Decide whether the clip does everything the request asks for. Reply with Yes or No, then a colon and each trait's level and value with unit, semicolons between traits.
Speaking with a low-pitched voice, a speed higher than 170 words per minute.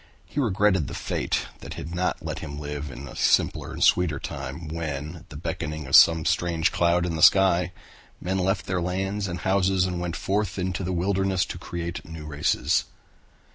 Yes: very low, 85 Hz; average, 190 wpm